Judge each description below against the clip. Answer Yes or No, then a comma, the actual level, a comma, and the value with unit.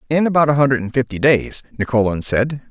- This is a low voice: Yes, low, 130 Hz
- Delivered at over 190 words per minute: Yes, average, 200 wpm